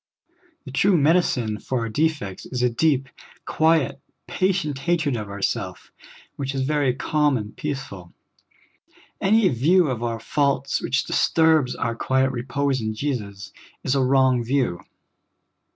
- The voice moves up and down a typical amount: Yes, average, 4.2 semitones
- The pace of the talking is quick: No, slow, 135 wpm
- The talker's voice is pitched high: No, low, 135 Hz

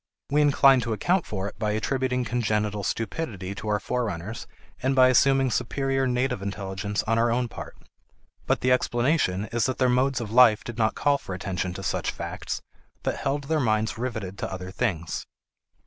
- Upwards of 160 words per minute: Yes, average, 180 wpm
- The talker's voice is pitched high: No, low, 115 Hz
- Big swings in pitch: No, average, 4.1 semitones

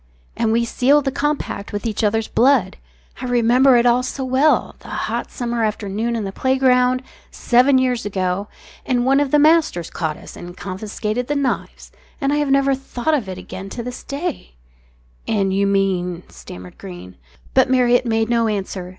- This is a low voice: No, high, 235 Hz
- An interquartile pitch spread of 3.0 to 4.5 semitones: No, average, 5.1 semitones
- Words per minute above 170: Yes, average, 185 wpm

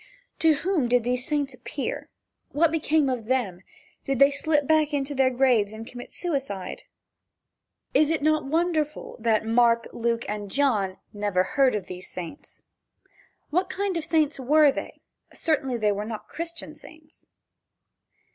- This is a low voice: No, very high, 270 Hz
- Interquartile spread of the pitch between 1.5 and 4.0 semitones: No, average, 5.2 semitones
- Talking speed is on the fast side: No, average, 150 wpm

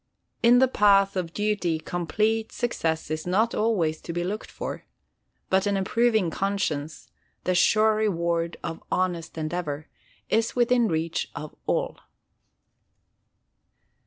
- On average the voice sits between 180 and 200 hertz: Yes, medium, 185 Hz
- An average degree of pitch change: Yes, average, 4.7 semitones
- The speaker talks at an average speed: No, slow, 125 wpm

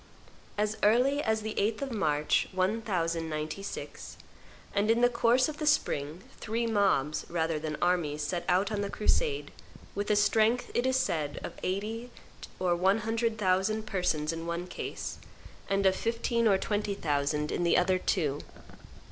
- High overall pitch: Yes, high, 200 Hz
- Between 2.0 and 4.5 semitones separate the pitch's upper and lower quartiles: No, average, 5.0 semitones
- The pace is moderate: Yes, average, 160 wpm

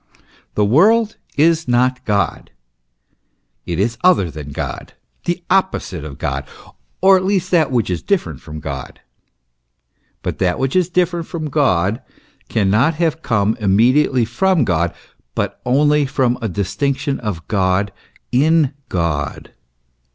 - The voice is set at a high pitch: No, low, 125 Hz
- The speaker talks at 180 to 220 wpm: No, slow, 135 wpm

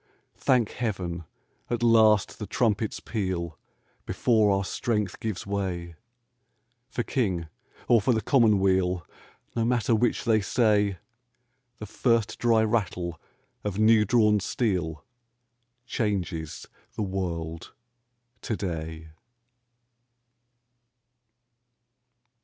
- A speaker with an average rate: No, slow, 95 wpm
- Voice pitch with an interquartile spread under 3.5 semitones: No, average, 4.0 semitones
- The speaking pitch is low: Yes, low, 105 Hz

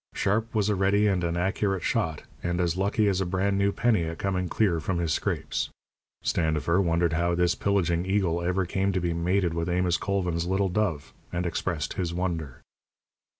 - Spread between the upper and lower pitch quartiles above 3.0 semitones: No, narrow, 2.5 semitones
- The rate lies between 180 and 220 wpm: Yes, average, 190 wpm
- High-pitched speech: No, very low, 90 Hz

